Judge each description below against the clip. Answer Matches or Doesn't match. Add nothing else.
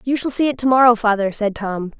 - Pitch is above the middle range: Matches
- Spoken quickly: Matches